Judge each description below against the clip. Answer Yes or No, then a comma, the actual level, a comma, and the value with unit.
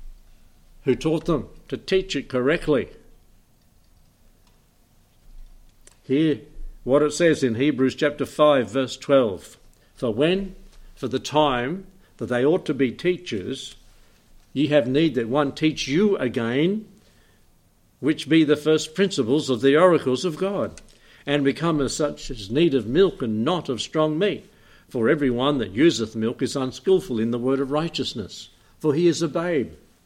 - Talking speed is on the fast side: No, average, 155 wpm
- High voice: No, medium, 140 Hz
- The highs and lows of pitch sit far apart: No, average, 4.5 semitones